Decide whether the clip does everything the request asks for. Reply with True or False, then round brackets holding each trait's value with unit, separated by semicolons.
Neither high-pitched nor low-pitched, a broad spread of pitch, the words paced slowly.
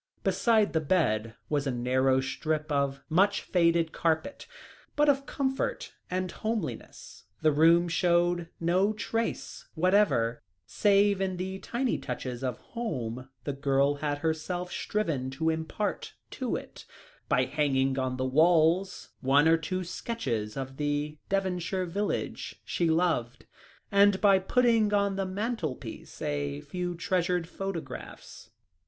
True (170 Hz; 5.7 semitones; 130 wpm)